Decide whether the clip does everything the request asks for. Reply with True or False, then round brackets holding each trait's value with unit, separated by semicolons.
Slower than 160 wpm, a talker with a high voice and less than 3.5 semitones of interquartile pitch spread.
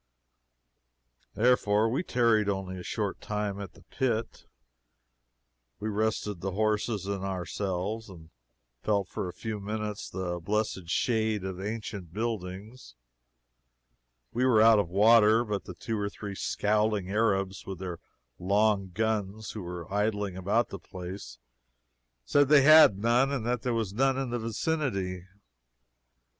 False (145 wpm; 105 Hz; 2.8 semitones)